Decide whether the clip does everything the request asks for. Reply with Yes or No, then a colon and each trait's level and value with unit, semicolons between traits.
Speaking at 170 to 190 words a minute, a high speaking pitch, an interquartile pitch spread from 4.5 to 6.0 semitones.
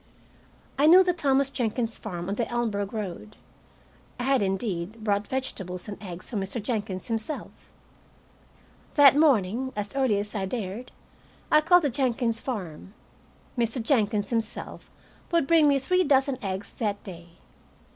No: average, 145 wpm; high, 225 Hz; average, 5.0 semitones